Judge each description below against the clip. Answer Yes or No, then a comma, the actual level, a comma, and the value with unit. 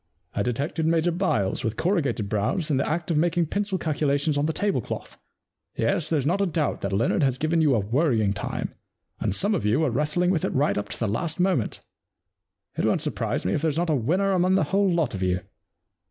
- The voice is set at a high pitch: No, medium, 155 Hz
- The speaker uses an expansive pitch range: Yes, wide, 6.3 semitones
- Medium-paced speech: No, fast, 220 wpm